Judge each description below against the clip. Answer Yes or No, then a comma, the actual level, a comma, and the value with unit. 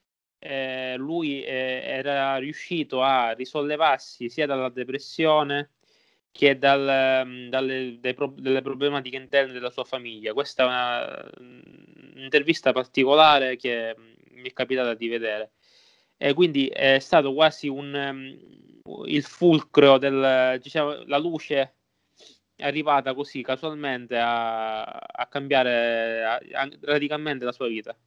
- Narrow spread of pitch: Yes, narrow, 2.1 semitones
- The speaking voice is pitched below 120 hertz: No, low, 135 Hz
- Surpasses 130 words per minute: No, average, 125 wpm